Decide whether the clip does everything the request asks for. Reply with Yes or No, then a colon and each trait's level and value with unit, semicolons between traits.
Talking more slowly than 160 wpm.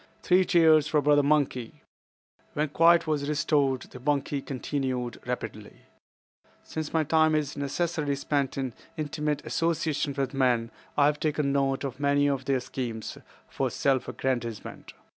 Yes: average, 140 wpm